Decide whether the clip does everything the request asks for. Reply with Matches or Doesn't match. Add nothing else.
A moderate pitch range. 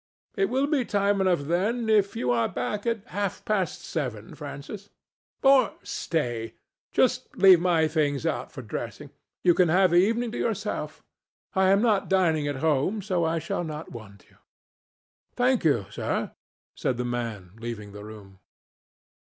Doesn't match